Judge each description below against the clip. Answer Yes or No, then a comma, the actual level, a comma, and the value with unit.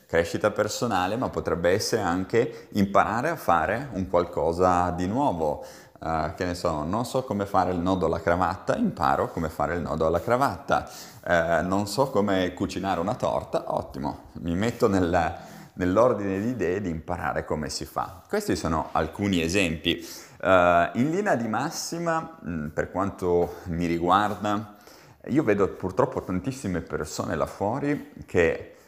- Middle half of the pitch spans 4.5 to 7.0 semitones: No, average, 3.9 semitones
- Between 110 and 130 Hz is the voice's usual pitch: No, very low, 95 Hz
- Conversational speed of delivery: Yes, average, 150 wpm